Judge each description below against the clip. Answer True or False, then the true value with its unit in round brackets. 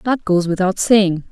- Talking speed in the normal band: True (180 wpm)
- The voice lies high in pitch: True (195 Hz)